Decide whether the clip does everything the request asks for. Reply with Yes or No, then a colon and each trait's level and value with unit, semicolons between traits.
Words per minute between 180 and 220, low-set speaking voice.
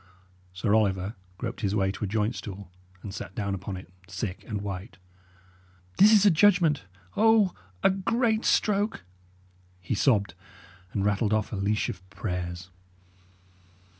No: average, 145 wpm; low, 105 Hz